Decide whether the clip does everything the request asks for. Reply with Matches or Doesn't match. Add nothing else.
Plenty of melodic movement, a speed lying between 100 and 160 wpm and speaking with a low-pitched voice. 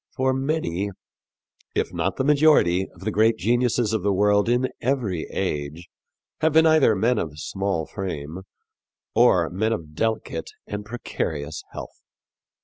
Matches